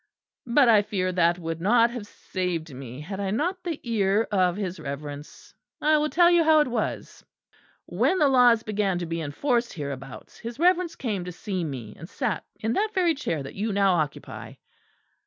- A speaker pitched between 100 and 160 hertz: No, high, 200 Hz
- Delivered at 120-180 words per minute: No, average, 190 wpm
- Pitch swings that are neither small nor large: No, wide, 7.1 semitones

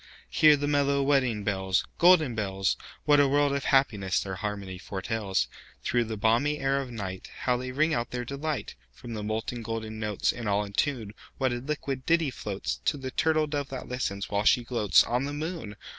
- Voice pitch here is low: Yes, low, 120 Hz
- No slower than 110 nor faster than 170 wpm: Yes, average, 165 wpm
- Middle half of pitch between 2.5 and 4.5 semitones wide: No, average, 5.1 semitones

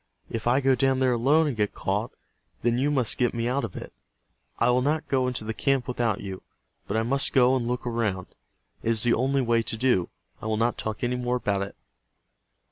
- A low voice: Yes, low, 120 Hz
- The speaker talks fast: Yes, fast, 225 wpm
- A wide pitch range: No, narrow, 2.6 semitones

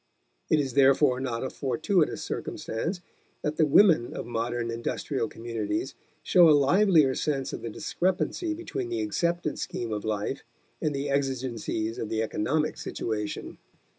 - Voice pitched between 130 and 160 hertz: Yes, low, 135 Hz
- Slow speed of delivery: No, average, 145 wpm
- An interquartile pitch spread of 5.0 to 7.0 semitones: Yes, wide, 5.5 semitones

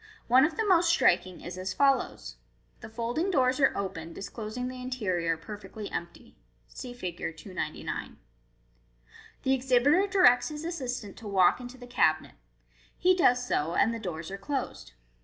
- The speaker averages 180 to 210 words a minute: No, average, 160 wpm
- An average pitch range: No, wide, 6.3 semitones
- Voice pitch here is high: Yes, high, 245 Hz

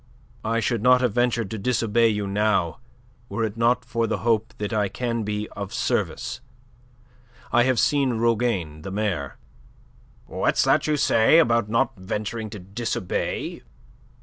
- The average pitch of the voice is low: Yes, low, 110 Hz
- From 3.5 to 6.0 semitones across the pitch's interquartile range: No, narrow, 2.5 semitones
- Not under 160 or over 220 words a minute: No, average, 150 wpm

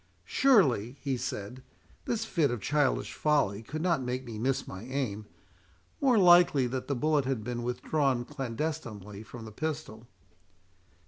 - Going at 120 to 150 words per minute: Yes, average, 140 wpm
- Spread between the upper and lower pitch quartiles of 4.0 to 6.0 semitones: Yes, wide, 5.5 semitones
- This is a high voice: No, low, 130 Hz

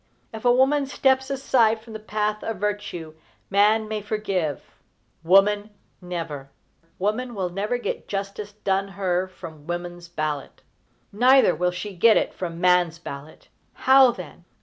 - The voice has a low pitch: No, high, 200 Hz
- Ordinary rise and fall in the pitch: Yes, average, 3.8 semitones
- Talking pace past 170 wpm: No, average, 145 wpm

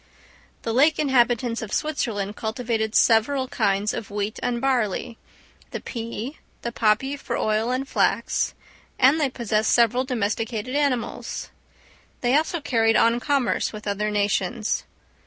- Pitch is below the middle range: No, high, 235 Hz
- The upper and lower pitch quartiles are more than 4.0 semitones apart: No, average, 3.3 semitones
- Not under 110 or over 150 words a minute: Yes, slow, 135 wpm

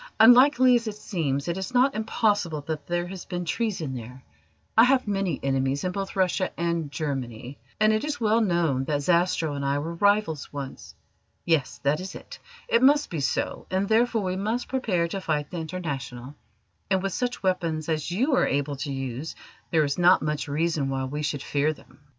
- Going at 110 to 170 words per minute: No, average, 195 wpm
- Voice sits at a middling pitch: Yes, medium, 170 Hz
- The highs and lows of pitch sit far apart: Yes, wide, 6.1 semitones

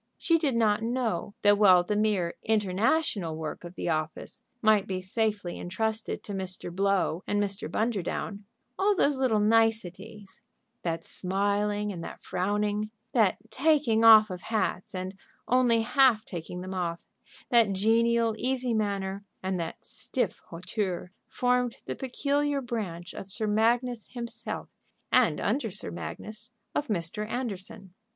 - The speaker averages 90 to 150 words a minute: Yes, average, 140 wpm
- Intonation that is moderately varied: Yes, average, 3.8 semitones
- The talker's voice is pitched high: Yes, high, 210 Hz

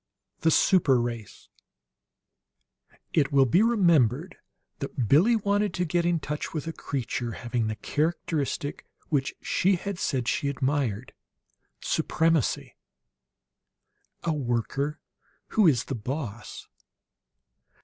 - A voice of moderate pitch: Yes, medium, 145 Hz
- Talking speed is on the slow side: Yes, slow, 115 wpm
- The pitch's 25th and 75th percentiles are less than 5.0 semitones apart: No, wide, 5.4 semitones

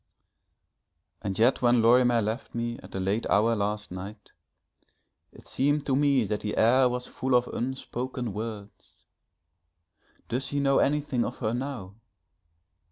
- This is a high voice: No, low, 120 Hz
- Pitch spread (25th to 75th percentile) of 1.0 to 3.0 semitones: No, average, 3.5 semitones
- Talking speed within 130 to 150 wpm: Yes, average, 145 wpm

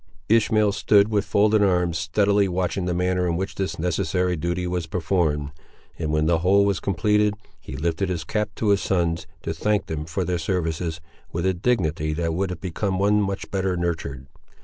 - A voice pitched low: Yes, very low, 90 Hz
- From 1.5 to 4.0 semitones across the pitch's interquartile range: Yes, average, 3.3 semitones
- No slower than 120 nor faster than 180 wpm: No, average, 190 wpm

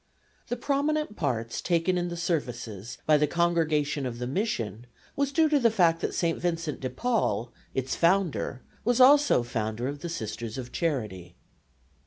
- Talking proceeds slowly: No, average, 165 wpm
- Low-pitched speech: No, medium, 160 Hz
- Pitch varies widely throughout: Yes, wide, 7.7 semitones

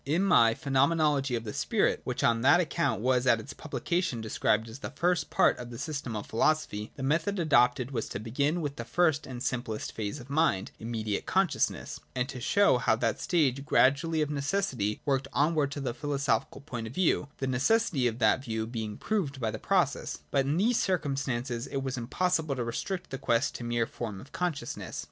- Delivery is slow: No, fast, 205 wpm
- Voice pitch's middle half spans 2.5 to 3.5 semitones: No, average, 4.7 semitones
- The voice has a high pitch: No, low, 135 Hz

